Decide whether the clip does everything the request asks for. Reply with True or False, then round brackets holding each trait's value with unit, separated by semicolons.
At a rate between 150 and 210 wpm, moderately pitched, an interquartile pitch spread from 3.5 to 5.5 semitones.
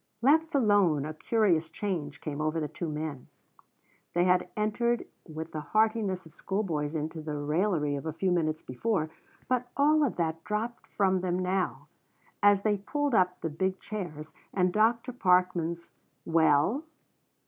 True (160 wpm; 180 Hz; 5.1 semitones)